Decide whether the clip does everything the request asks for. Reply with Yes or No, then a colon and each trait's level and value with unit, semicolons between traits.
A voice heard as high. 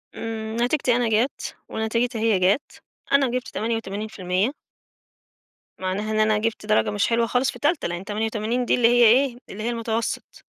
Yes: high, 225 Hz